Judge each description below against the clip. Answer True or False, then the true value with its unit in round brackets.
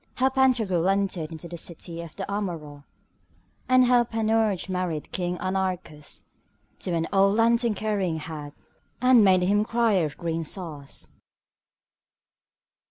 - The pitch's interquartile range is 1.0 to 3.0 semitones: False (4.8 semitones)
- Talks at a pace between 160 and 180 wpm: False (135 wpm)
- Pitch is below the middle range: False (185 Hz)